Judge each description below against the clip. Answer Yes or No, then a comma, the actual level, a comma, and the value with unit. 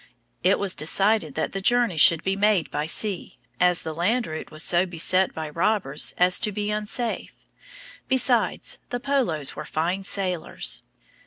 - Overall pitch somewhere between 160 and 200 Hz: Yes, medium, 185 Hz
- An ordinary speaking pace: Yes, average, 160 wpm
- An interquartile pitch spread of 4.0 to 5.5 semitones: Yes, average, 4.8 semitones